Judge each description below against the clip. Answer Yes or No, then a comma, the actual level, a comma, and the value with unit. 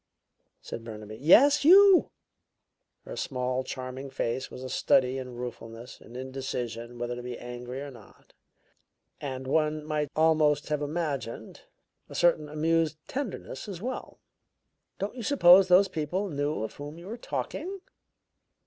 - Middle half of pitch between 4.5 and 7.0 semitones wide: Yes, wide, 5.5 semitones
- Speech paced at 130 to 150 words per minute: Yes, average, 140 wpm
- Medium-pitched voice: Yes, medium, 145 Hz